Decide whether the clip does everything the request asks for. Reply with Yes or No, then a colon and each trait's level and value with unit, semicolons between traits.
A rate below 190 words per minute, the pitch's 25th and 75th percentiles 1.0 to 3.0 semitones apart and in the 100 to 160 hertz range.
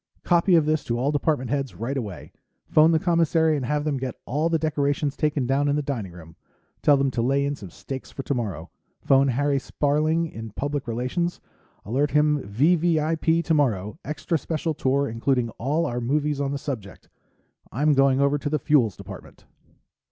No: average, 180 wpm; average, 3.5 semitones; medium, 140 Hz